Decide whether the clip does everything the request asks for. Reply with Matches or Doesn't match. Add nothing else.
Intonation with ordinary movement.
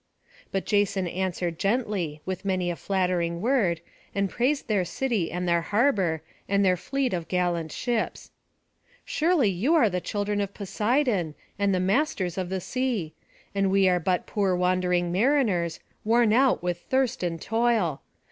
Matches